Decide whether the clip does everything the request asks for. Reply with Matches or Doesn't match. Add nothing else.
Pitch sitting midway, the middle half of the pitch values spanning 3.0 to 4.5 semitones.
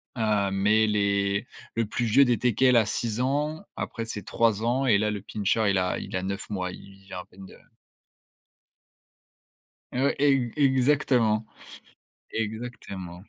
Doesn't match